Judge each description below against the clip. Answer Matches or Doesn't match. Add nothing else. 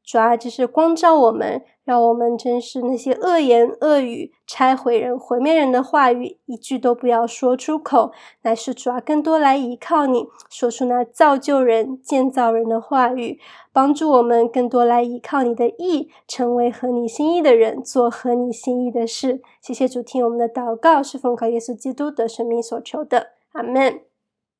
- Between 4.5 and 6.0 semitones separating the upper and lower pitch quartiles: Doesn't match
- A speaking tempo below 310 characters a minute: Matches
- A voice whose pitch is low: Doesn't match